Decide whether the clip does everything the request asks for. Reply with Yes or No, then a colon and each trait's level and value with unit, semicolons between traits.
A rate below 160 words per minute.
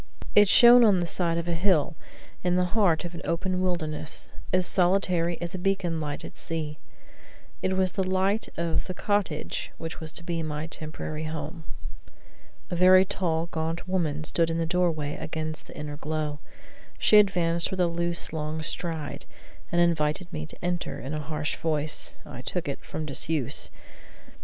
No: average, 175 wpm